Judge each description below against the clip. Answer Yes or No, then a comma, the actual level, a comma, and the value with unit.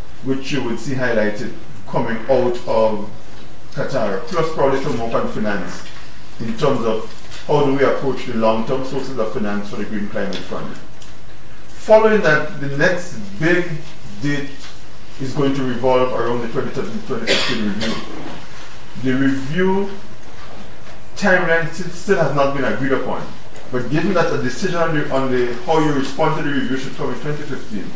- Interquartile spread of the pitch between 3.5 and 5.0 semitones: Yes, average, 4.2 semitones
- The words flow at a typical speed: Yes, average, 160 wpm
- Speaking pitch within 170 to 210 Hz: No, low, 135 Hz